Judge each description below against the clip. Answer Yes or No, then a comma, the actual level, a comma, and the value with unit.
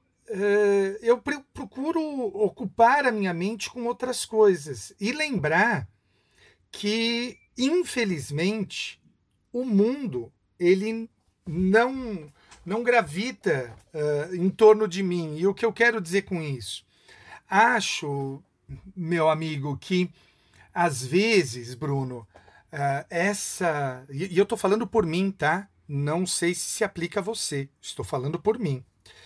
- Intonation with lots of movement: Yes, wide, 7.2 semitones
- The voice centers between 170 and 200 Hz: Yes, medium, 185 Hz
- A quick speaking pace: No, average, 125 wpm